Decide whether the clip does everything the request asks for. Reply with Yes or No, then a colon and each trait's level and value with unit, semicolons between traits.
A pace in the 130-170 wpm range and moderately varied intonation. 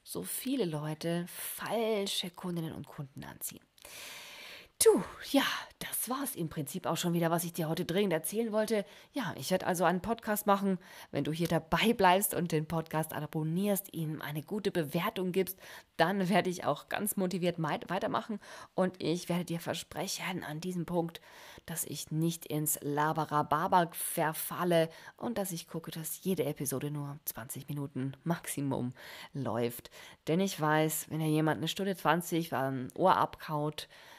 Yes: average, 160 wpm; average, 3.5 semitones